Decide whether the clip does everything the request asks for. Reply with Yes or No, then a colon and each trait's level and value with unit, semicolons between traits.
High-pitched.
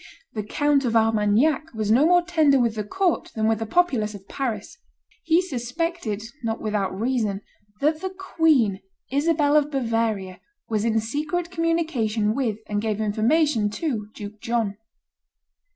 Yes: high, 235 Hz